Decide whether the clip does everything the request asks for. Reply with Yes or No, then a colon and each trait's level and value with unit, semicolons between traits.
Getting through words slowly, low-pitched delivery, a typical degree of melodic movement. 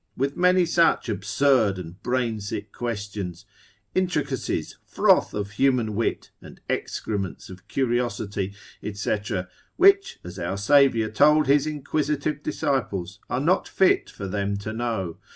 No: slow, 130 wpm; low, 115 Hz; wide, 6.1 semitones